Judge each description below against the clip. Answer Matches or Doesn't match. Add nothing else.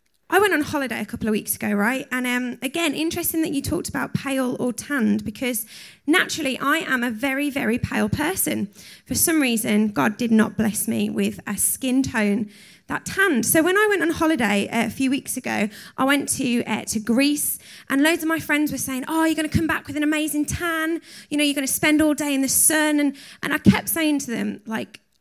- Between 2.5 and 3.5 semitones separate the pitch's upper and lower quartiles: Doesn't match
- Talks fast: Matches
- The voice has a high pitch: Matches